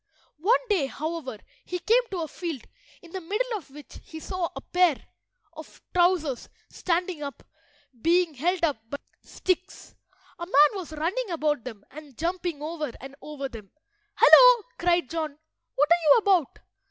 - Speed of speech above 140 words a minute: Yes, average, 160 wpm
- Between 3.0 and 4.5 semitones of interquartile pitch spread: Yes, average, 3.7 semitones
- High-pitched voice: Yes, very high, 330 Hz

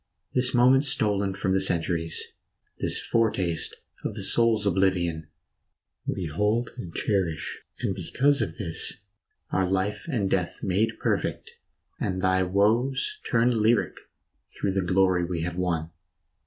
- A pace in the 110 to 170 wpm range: Yes, slow, 135 wpm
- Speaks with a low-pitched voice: Yes, very low, 95 Hz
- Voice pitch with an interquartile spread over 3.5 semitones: Yes, average, 4.2 semitones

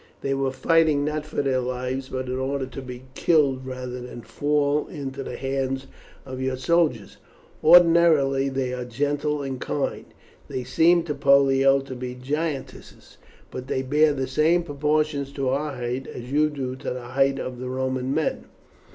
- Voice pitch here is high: No, low, 135 Hz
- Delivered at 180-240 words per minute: No, average, 170 wpm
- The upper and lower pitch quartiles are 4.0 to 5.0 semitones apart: No, narrow, 2.4 semitones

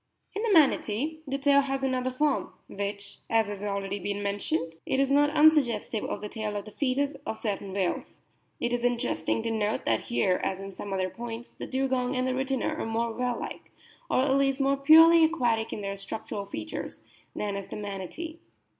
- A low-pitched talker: No, high, 235 Hz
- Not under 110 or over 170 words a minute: No, average, 195 wpm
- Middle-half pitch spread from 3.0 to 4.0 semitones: No, average, 5.2 semitones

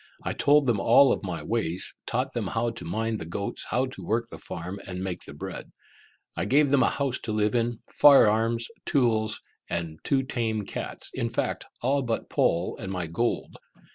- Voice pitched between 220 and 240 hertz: No, low, 115 Hz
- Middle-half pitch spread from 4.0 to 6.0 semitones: Yes, average, 4.9 semitones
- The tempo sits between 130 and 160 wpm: No, average, 200 wpm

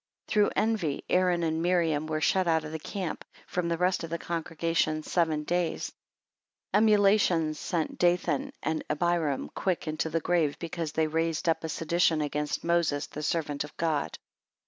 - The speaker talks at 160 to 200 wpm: Yes, average, 170 wpm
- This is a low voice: No, medium, 165 Hz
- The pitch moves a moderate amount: No, narrow, 2.1 semitones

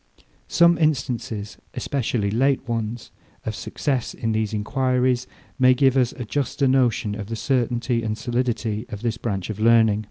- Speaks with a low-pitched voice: Yes, low, 120 Hz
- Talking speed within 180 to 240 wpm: No, average, 155 wpm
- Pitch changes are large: No, average, 2.8 semitones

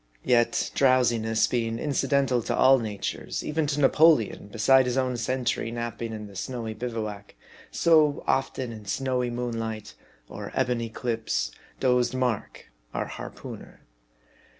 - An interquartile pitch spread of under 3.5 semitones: Yes, average, 2.7 semitones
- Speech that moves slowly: Yes, slow, 130 wpm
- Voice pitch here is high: No, low, 120 Hz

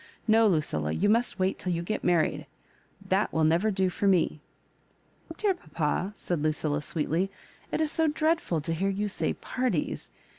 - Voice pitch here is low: No, medium, 185 Hz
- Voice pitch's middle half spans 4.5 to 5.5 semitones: Yes, average, 5.2 semitones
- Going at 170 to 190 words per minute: Yes, average, 180 wpm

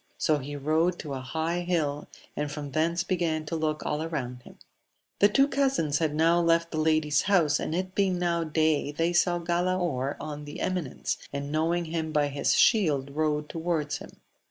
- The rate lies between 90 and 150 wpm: No, average, 190 wpm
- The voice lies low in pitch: No, medium, 160 Hz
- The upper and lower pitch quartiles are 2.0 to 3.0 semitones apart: Yes, average, 2.7 semitones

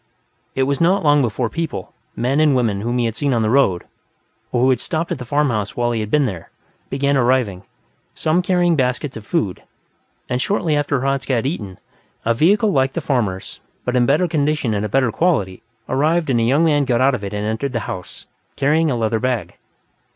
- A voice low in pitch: Yes, low, 130 Hz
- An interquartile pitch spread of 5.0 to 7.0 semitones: No, average, 4.5 semitones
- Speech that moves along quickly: Yes, fast, 210 wpm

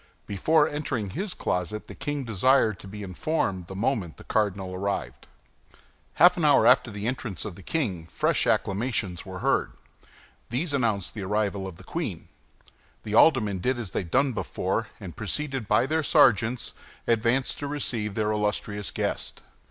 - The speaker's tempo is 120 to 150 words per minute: No, average, 165 wpm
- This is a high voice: No, low, 110 Hz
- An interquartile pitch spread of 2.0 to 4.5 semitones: No, average, 5.3 semitones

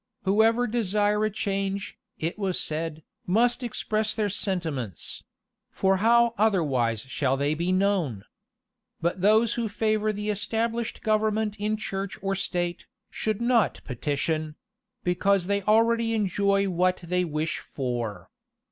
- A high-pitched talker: Yes, high, 195 Hz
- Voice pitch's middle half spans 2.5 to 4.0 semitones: No, average, 4.4 semitones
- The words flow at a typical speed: No, slow, 130 wpm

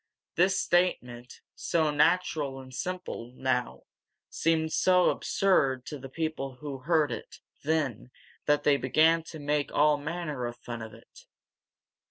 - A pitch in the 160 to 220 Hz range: No, medium, 150 Hz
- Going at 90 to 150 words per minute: Yes, average, 140 wpm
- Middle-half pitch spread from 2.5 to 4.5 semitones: Yes, average, 3.9 semitones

